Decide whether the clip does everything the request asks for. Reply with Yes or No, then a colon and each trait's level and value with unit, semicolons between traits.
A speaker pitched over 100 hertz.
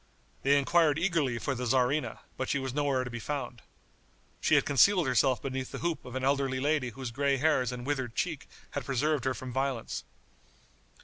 Yes: low, 135 Hz